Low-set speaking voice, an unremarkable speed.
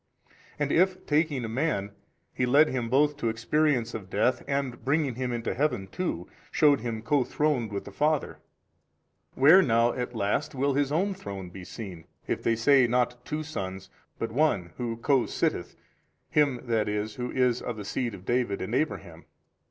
Yes: low, 125 Hz; average, 185 wpm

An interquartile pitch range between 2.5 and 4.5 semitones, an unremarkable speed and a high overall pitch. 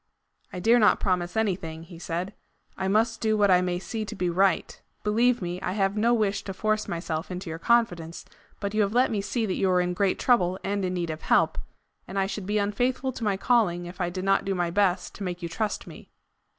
No: average, 3.2 semitones; fast, 240 wpm; high, 195 Hz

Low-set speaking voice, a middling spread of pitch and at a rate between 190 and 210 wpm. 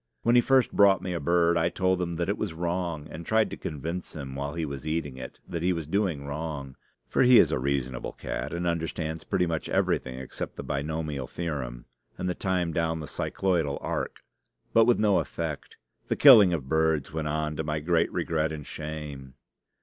Yes: very low, 80 Hz; average, 3.3 semitones; fast, 205 wpm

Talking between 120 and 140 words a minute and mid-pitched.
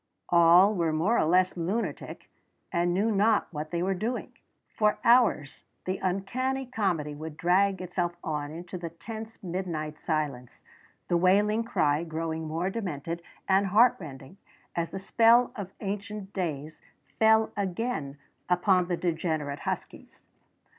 Yes: slow, 135 wpm; medium, 180 Hz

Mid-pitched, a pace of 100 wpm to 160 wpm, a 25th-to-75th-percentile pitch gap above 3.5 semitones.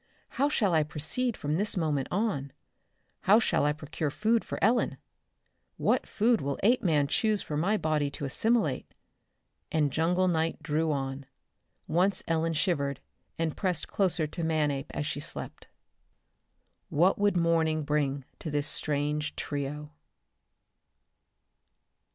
Yes: medium, 155 Hz; slow, 135 wpm; average, 4.2 semitones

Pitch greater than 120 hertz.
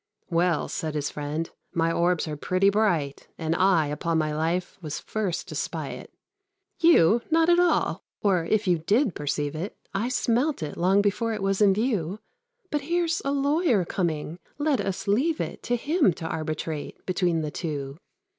Yes: medium, 185 Hz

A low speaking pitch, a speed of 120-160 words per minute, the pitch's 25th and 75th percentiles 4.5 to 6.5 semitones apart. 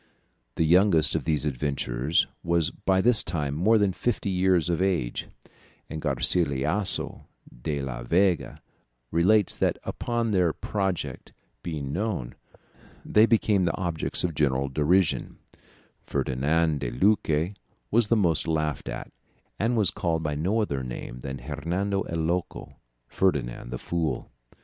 Yes: very low, 85 Hz; slow, 135 wpm; average, 4.9 semitones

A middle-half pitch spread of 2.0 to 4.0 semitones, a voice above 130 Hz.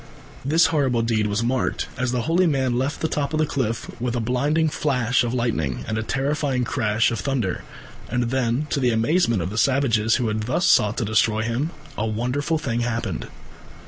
No: average, 3.7 semitones; low, 125 Hz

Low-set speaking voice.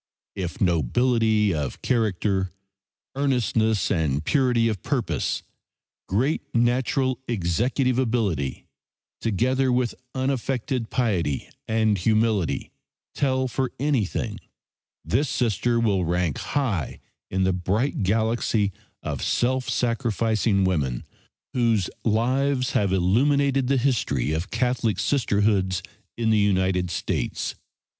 Yes: low, 110 Hz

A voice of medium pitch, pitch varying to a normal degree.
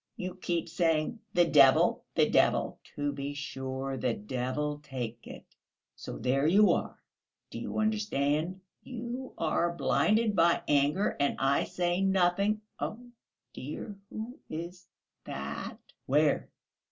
No: medium, 165 Hz; wide, 5.8 semitones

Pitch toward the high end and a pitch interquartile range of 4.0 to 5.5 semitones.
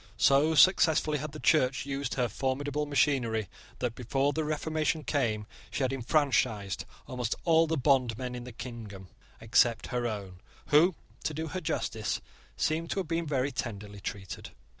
No: low, 135 Hz; average, 4.8 semitones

